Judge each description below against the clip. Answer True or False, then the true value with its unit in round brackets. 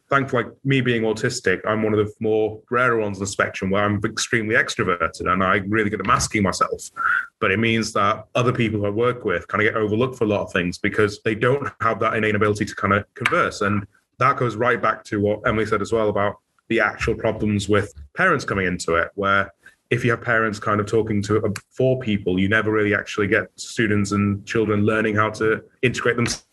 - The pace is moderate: False (225 wpm)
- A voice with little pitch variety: True (1.8 semitones)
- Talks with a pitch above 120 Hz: False (110 Hz)